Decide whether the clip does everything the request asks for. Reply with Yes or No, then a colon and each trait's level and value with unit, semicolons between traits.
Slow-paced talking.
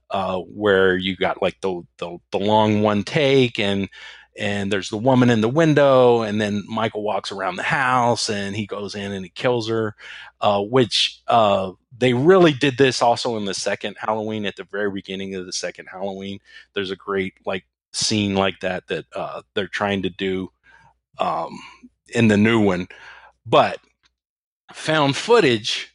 No: average, 175 wpm